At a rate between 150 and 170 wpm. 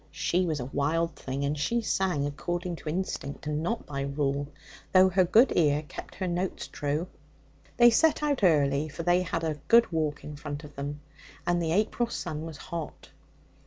No: average, 190 wpm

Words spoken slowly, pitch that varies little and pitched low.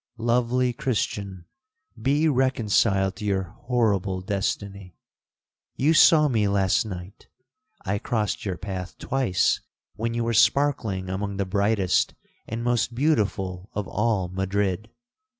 No: slow, 115 wpm; average, 4.0 semitones; low, 105 Hz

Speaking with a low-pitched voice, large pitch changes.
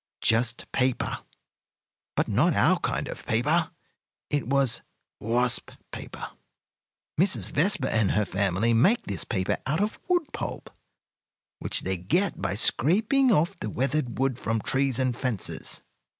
Yes: low, 130 Hz; wide, 5.7 semitones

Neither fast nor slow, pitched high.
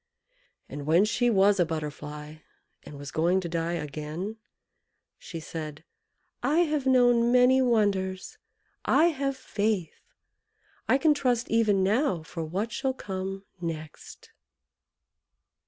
No: slow, 125 wpm; high, 195 Hz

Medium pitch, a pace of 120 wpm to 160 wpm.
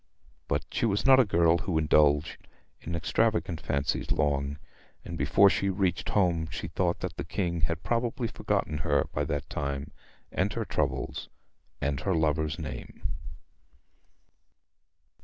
No: very low, 80 Hz; average, 140 wpm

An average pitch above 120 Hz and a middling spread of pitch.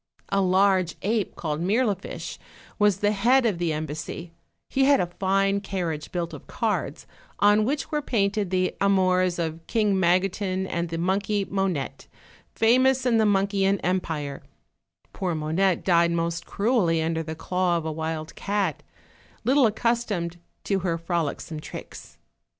Yes: medium, 185 Hz; average, 3.4 semitones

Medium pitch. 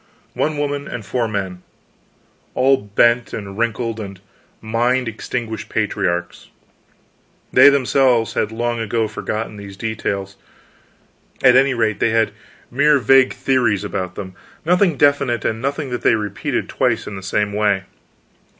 No: low, 115 Hz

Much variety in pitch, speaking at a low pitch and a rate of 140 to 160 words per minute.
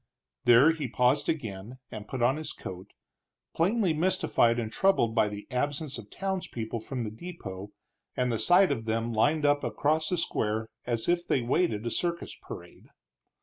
No: wide, 6.4 semitones; low, 125 Hz; average, 170 wpm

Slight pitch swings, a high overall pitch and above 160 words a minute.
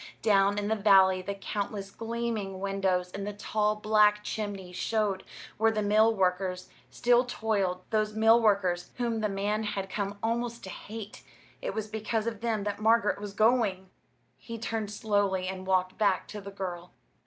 Yes: narrow, 2.2 semitones; high, 205 Hz; average, 170 wpm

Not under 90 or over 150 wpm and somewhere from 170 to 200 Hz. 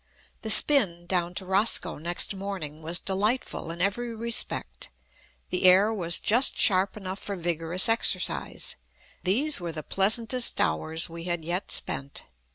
Yes: average, 145 wpm; medium, 185 Hz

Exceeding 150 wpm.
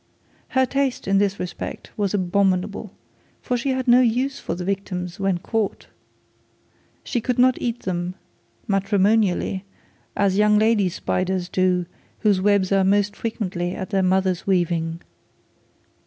No: average, 140 wpm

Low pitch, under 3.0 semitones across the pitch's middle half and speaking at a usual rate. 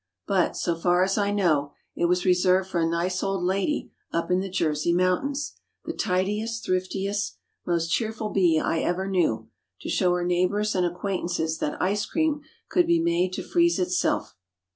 No: medium, 185 Hz; narrow, 2.5 semitones; average, 165 wpm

